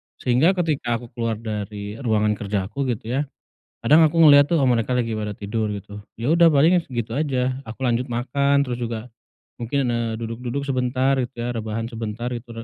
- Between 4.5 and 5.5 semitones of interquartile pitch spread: No, average, 3.7 semitones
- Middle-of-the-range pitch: No, low, 120 Hz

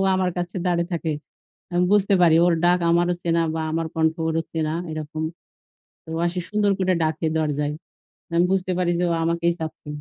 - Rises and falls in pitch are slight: Yes, narrow, 1.8 semitones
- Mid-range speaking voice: Yes, medium, 170 Hz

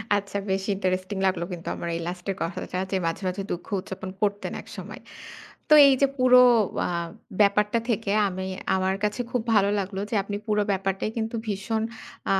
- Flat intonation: Yes, narrow, 1.9 semitones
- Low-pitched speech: No, high, 195 Hz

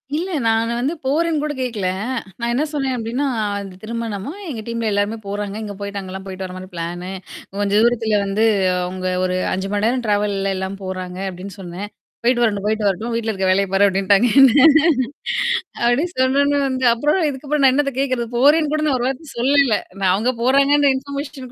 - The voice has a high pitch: Yes, high, 230 Hz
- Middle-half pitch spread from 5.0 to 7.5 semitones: Yes, wide, 5.4 semitones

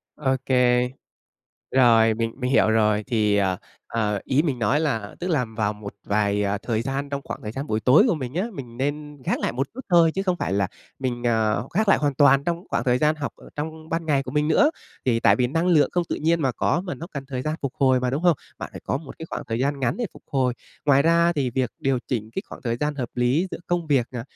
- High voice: No, low, 135 Hz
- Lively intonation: No, average, 4.7 semitones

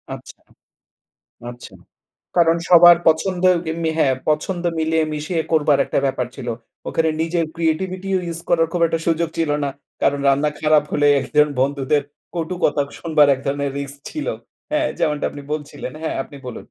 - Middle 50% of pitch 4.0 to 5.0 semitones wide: No, average, 2.7 semitones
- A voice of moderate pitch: Yes, medium, 160 Hz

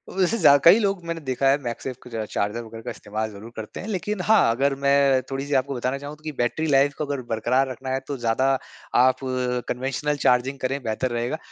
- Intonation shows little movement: No, average, 3.2 semitones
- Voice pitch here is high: No, low, 135 Hz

